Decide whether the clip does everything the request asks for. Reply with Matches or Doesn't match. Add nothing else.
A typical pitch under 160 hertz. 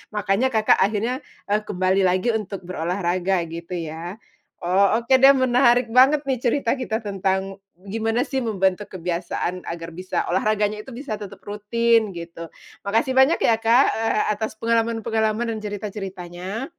Doesn't match